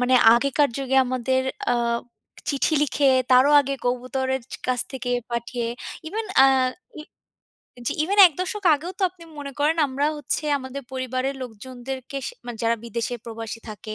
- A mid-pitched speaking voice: No, very high, 260 Hz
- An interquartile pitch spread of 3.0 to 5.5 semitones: No, narrow, 2.5 semitones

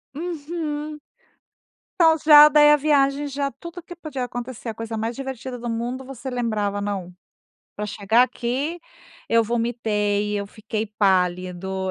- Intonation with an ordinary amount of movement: No, wide, 5.8 semitones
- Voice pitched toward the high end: Yes, high, 240 Hz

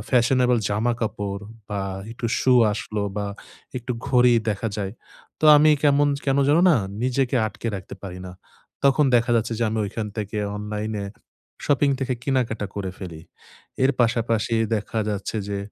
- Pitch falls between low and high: No, low, 115 Hz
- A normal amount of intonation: Yes, average, 3.7 semitones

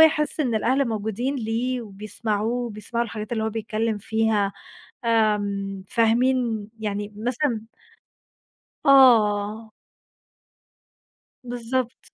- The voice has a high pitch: Yes, high, 225 Hz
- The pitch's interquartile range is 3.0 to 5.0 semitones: No, narrow, 2.5 semitones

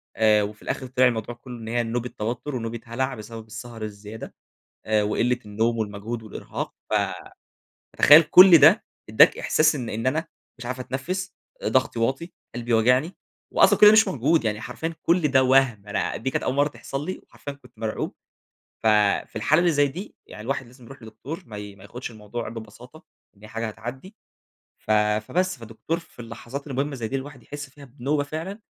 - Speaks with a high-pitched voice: No, low, 125 Hz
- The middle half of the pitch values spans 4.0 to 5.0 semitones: Yes, average, 4.4 semitones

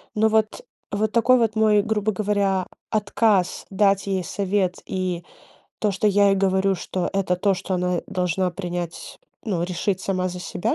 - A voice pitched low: No, high, 195 Hz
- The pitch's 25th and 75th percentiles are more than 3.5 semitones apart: No, narrow, 2.4 semitones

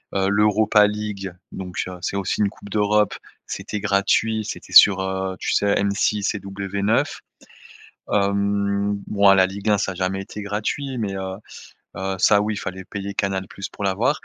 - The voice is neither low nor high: No, low, 100 Hz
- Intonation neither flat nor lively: No, narrow, 1.3 semitones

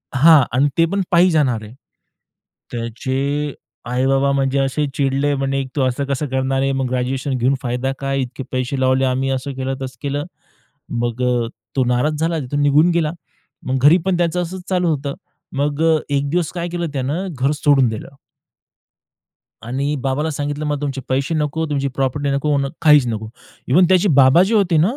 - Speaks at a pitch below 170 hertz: Yes, medium, 140 Hz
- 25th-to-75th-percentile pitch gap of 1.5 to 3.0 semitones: Yes, narrow, 2.5 semitones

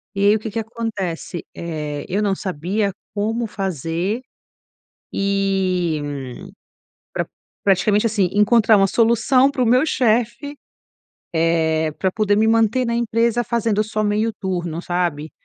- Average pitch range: Yes, average, 4.3 semitones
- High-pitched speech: Yes, high, 205 Hz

